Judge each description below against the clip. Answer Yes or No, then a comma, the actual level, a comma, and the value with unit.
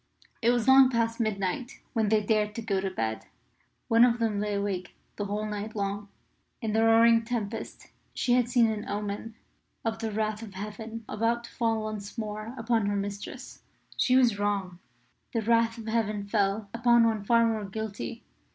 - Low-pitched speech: No, high, 220 Hz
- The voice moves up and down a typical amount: No, narrow, 2.1 semitones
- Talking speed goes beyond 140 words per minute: Yes, average, 180 wpm